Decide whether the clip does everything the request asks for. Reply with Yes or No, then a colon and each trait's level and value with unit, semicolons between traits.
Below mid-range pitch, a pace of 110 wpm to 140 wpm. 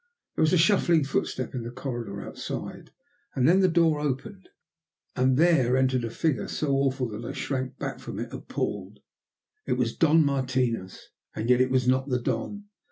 No: low, 130 Hz; average, 180 wpm